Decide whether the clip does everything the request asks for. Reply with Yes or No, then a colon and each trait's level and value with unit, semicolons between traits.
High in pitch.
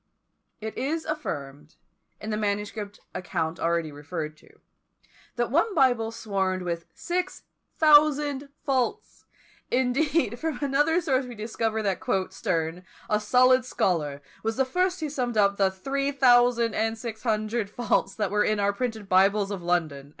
Yes: high, 220 Hz